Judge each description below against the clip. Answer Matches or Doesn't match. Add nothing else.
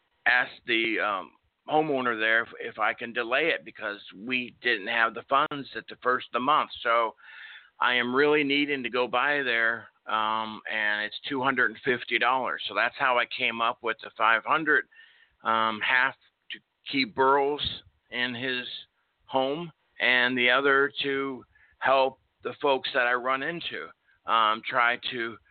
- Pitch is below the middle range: Matches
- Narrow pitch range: Doesn't match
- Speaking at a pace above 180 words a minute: Doesn't match